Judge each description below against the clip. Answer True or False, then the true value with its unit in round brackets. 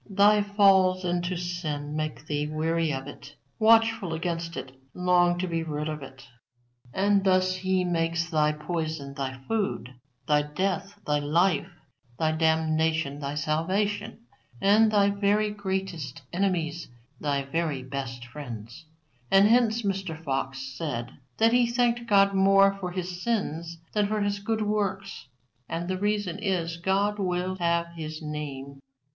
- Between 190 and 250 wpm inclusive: False (145 wpm)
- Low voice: False (175 Hz)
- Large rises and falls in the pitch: False (4.6 semitones)